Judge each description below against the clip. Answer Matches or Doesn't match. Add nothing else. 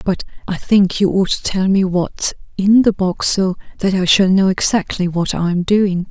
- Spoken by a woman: Matches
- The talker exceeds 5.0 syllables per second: Doesn't match